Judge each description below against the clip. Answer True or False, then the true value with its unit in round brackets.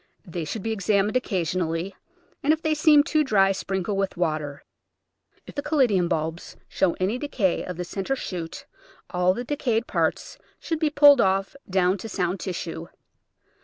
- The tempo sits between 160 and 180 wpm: True (165 wpm)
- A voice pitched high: True (195 Hz)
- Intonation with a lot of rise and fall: True (6.1 semitones)